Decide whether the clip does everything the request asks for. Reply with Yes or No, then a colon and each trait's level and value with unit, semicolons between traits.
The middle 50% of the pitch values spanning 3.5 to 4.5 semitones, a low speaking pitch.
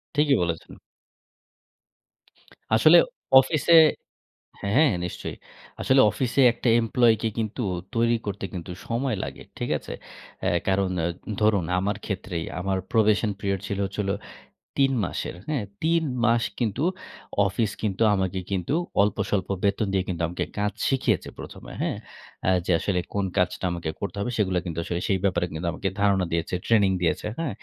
Yes: average, 3.8 semitones; low, 100 Hz